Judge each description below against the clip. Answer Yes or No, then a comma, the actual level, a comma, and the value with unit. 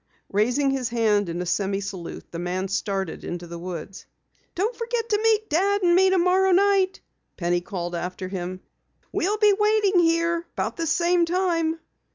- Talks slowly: No, average, 170 wpm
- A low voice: No, very high, 325 Hz